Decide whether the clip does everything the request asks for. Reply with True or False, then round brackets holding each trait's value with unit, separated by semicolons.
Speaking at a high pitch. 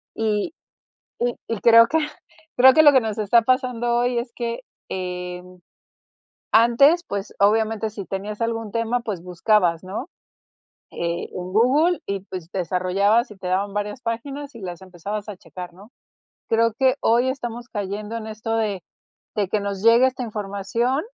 True (220 Hz)